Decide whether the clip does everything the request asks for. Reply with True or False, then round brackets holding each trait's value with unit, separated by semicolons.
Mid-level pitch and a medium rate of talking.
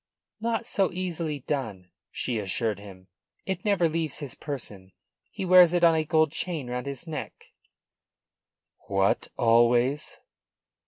False (145 Hz; 130 wpm)